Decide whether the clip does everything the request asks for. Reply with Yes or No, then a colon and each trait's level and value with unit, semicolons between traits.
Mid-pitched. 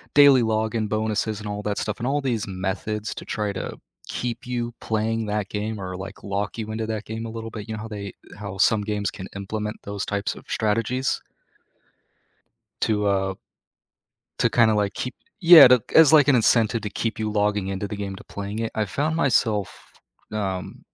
No: low, 110 Hz